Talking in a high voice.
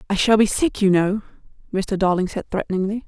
Yes: high, 200 Hz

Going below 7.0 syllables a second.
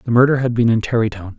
No: 7.2 syllables/s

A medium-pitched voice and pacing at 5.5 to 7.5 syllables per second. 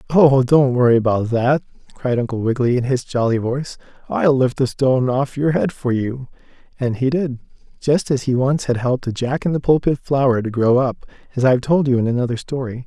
No: low, 130 Hz; 5.6 syllables/s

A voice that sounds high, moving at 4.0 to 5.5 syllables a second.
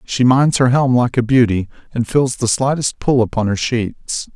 No: low, 120 Hz; 4.5 syllables/s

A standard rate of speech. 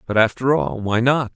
No: fast, 220 wpm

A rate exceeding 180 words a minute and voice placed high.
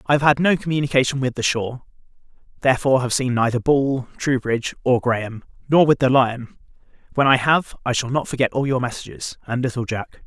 No: average, 195 wpm; low, 130 Hz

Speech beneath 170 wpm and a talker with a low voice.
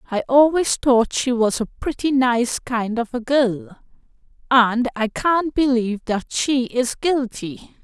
No: average, 155 wpm; very high, 250 Hz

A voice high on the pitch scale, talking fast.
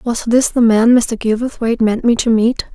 Yes: high, 230 Hz; fast, 220 wpm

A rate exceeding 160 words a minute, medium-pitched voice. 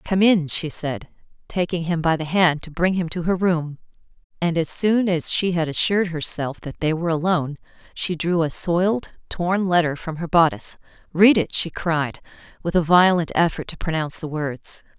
Yes: average, 190 wpm; medium, 170 Hz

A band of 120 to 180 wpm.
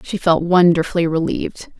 Yes: slow, 135 wpm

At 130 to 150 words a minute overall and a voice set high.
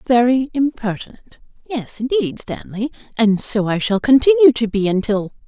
Yes: average, 140 wpm; high, 235 Hz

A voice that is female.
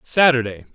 No: male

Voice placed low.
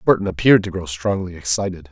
Yes: very low, 90 Hz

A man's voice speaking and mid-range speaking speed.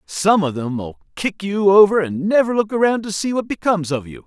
No: male; fast, 240 wpm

